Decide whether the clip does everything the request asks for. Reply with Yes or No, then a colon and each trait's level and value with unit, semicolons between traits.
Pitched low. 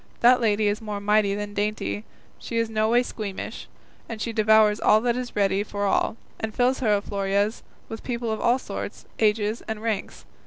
No: high, 215 Hz